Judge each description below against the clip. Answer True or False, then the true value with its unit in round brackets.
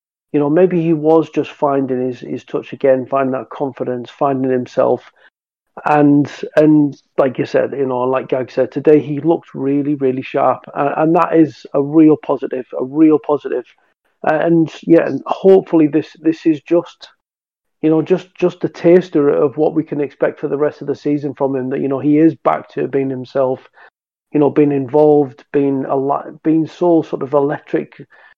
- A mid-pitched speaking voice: True (145 Hz)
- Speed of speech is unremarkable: True (190 wpm)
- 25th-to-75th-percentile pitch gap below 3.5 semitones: True (2.5 semitones)